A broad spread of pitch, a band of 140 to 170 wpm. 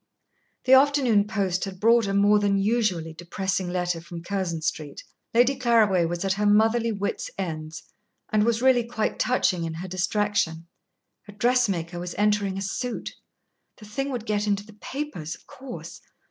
No: average, 4.4 semitones; average, 165 wpm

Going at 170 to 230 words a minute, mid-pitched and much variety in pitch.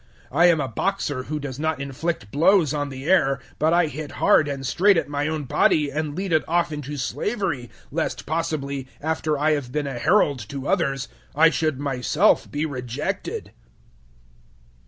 No: average, 175 wpm; medium, 150 Hz; narrow, 2.6 semitones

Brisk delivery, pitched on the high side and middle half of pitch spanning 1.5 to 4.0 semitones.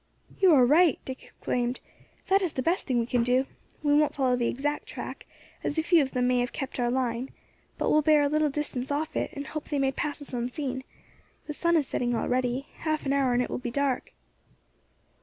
Yes: fast, 225 wpm; very high, 275 Hz; average, 3.3 semitones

